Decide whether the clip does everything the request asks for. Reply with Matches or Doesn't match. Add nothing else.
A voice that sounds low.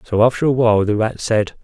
Matches